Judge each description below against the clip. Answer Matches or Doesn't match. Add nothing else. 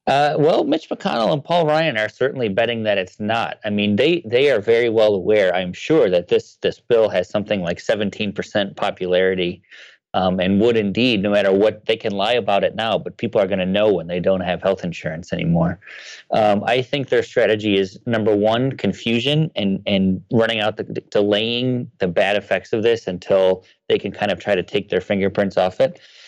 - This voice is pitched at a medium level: Doesn't match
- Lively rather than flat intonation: Matches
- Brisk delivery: Matches